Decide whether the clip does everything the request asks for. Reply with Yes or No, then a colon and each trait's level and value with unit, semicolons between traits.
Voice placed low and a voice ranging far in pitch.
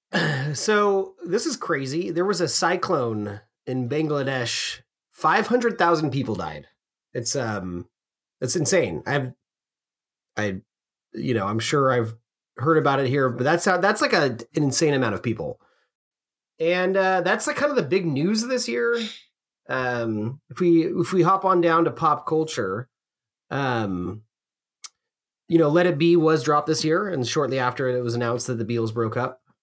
No: medium, 145 Hz; wide, 6.4 semitones